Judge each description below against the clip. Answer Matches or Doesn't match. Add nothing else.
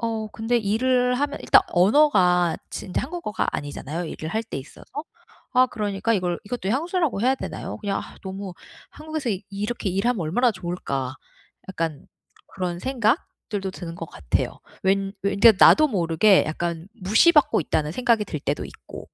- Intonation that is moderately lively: Doesn't match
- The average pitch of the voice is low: Doesn't match